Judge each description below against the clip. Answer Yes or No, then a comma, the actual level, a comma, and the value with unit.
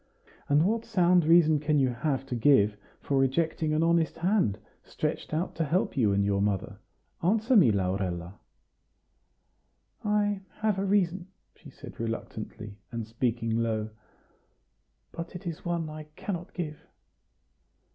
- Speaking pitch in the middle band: Yes, medium, 150 Hz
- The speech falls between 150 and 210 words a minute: No, average, 140 wpm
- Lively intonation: Yes, wide, 7.7 semitones